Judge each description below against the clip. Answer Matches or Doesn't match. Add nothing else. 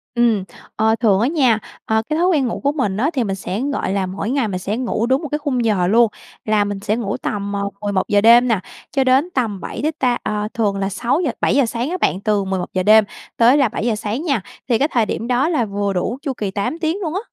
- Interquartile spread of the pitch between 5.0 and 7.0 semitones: Doesn't match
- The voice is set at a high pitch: Matches